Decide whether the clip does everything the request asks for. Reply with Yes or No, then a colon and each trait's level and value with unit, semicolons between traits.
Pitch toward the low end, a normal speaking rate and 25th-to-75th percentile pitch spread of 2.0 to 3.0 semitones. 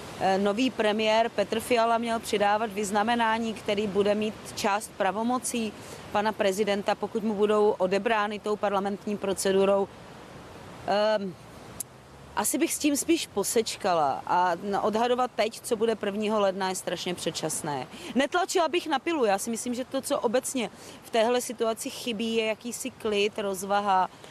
No: high, 215 Hz; average, 140 wpm; narrow, 2.6 semitones